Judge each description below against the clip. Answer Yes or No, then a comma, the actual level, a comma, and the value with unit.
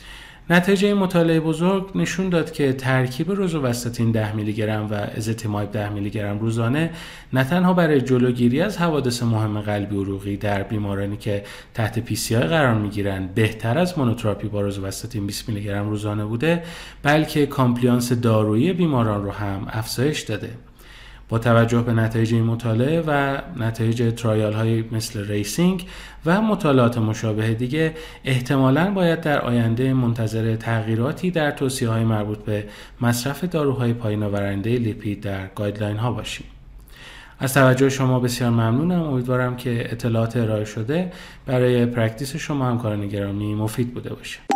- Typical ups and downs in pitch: Yes, average, 4.7 semitones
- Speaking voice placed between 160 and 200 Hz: No, low, 120 Hz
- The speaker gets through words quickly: No, average, 145 wpm